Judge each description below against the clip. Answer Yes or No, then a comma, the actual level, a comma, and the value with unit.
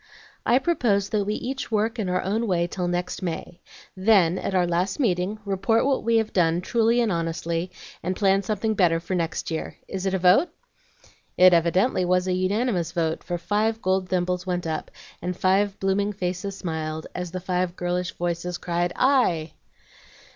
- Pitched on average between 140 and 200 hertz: Yes, medium, 185 Hz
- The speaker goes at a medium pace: Yes, average, 180 wpm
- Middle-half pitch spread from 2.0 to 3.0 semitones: Yes, average, 2.7 semitones